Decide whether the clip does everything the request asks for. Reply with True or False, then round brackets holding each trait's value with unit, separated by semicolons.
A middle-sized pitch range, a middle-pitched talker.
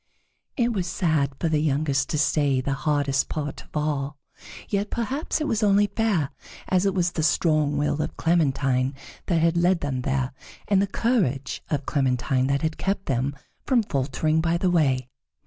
True (5.0 semitones; 155 Hz)